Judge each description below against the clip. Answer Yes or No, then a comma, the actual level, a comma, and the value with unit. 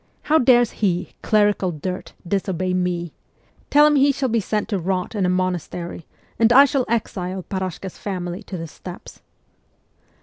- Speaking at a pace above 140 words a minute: Yes, average, 160 wpm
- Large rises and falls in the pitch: No, average, 4.2 semitones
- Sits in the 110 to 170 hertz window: No, high, 190 Hz